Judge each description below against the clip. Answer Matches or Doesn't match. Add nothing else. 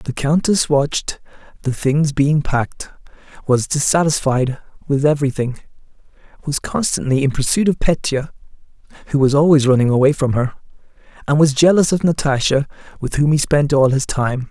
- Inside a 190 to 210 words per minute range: Doesn't match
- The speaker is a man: Matches